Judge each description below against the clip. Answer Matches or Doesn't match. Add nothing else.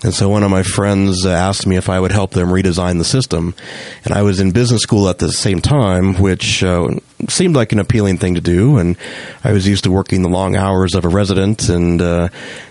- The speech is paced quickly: Matches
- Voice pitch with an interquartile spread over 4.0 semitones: Doesn't match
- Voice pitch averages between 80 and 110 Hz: Matches